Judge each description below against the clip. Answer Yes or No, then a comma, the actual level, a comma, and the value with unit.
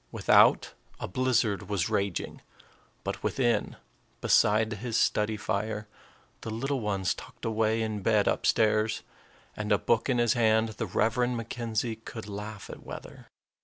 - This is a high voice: No, low, 110 Hz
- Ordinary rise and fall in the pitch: No, narrow, 1.6 semitones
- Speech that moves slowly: No, average, 145 wpm